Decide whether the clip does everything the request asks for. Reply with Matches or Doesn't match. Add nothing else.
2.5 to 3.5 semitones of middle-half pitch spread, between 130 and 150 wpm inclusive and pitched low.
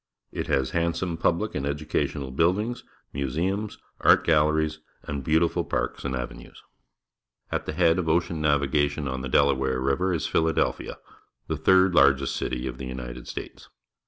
Doesn't match